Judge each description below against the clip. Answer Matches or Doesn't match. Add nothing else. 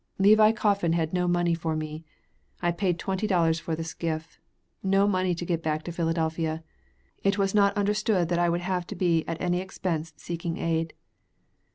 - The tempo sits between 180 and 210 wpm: Matches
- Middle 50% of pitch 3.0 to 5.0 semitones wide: Doesn't match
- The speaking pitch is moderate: Matches